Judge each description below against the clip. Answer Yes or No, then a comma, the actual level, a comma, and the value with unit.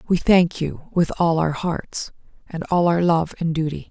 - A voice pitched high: No, medium, 165 Hz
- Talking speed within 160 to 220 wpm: Yes, average, 200 wpm